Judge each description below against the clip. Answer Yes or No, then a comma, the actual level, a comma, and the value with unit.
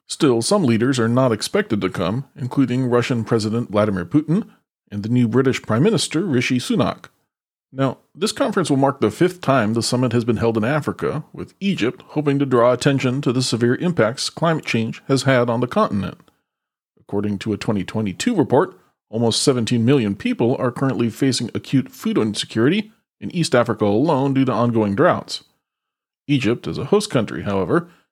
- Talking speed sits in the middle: Yes, average, 175 wpm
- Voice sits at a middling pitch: No, low, 125 Hz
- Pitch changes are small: No, average, 4.0 semitones